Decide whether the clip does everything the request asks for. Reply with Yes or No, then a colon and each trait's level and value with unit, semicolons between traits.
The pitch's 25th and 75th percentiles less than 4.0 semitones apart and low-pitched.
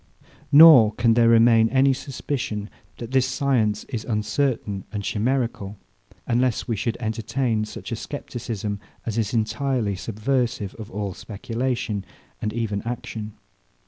Yes: average, 3.1 semitones; low, 115 Hz